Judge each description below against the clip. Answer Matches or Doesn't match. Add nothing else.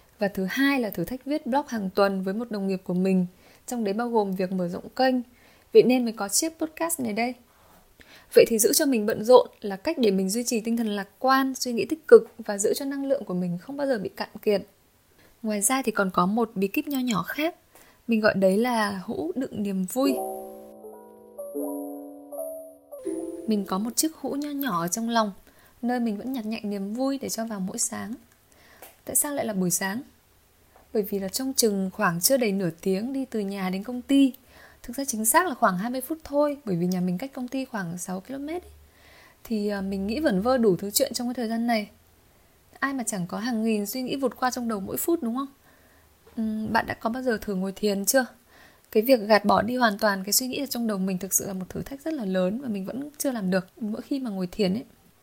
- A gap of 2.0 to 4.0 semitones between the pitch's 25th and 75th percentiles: Doesn't match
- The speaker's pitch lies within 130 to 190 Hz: Doesn't match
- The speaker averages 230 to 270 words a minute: Matches